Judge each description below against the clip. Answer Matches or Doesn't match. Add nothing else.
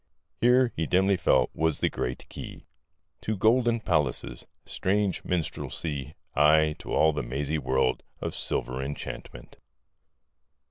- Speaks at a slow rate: Matches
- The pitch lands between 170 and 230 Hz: Doesn't match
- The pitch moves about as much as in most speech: Doesn't match